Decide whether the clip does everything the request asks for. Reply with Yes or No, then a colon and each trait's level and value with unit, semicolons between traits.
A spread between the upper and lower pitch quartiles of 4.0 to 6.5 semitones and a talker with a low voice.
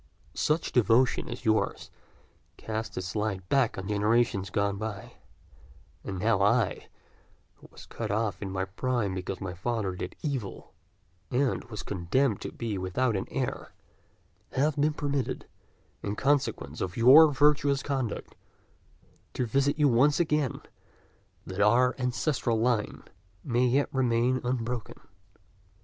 Yes: average, 4.6 semitones; low, 115 Hz